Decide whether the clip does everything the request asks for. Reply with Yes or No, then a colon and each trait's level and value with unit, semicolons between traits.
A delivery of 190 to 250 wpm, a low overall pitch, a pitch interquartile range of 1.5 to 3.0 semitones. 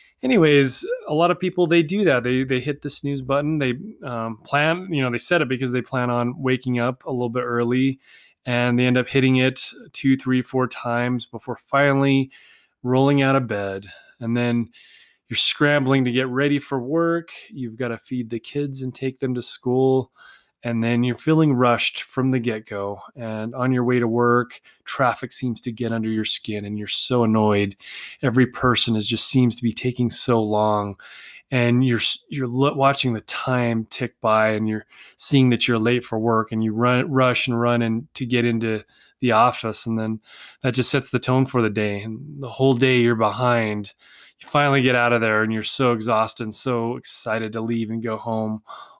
Yes: average, 200 wpm; low, 125 Hz; narrow, 2.6 semitones